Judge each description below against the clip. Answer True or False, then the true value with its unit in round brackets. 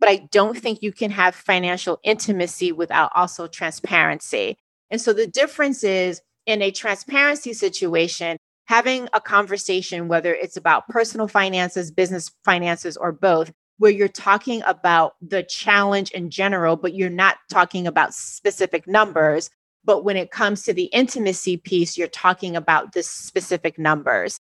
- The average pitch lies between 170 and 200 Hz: True (190 Hz)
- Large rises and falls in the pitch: False (3.3 semitones)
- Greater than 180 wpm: False (150 wpm)